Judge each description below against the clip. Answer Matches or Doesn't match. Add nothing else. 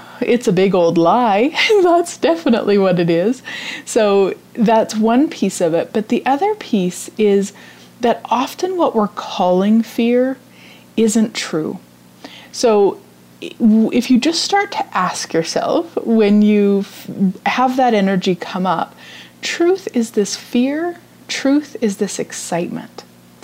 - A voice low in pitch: Doesn't match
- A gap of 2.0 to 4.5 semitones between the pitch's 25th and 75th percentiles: Doesn't match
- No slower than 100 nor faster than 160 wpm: Matches